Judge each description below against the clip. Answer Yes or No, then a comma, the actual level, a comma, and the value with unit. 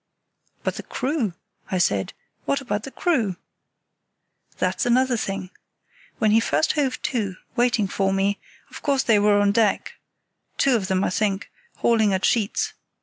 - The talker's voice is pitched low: No, high, 215 Hz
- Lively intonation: No, average, 4.1 semitones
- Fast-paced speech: No, average, 155 wpm